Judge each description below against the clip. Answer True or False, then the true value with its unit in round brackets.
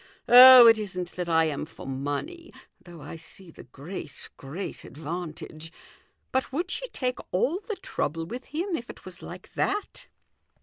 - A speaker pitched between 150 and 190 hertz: True (185 Hz)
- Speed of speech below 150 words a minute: False (165 wpm)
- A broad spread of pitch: True (8.4 semitones)